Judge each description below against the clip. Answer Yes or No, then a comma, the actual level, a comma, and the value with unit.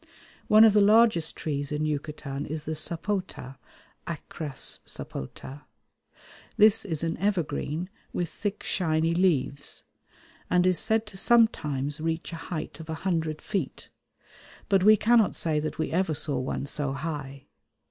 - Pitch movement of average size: Yes, average, 4.5 semitones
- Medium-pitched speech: Yes, medium, 160 Hz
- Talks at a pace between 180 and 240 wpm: No, average, 145 wpm